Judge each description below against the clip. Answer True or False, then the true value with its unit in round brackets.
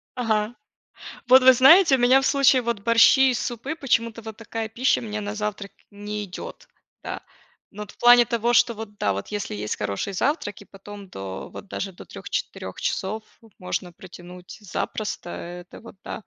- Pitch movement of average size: True (3.7 semitones)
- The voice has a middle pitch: False (215 Hz)